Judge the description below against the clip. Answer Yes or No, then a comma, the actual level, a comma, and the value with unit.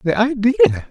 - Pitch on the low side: No, high, 195 Hz